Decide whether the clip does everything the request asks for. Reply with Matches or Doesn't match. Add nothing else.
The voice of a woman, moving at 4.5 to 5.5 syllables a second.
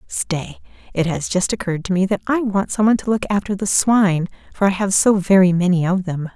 Doesn't match